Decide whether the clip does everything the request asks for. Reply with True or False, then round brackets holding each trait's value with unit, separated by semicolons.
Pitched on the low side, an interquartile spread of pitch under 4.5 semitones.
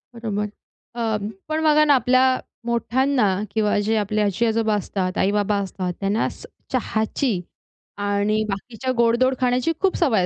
False (225 Hz; 3.8 semitones)